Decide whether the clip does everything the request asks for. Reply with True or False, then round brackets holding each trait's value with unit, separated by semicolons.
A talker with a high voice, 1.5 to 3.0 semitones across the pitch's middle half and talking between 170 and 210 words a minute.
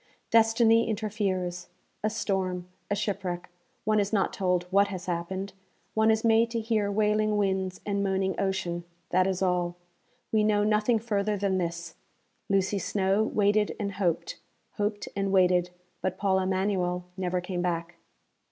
False (195 Hz; 2.6 semitones; 150 wpm)